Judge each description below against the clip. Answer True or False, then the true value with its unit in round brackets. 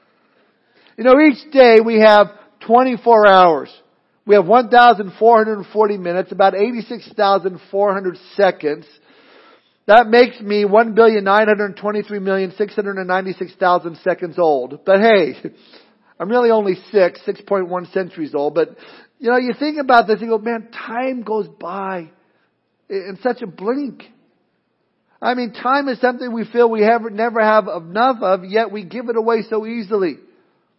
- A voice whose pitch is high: True (215 Hz)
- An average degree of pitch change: True (3.5 semitones)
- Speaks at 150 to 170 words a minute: False (135 wpm)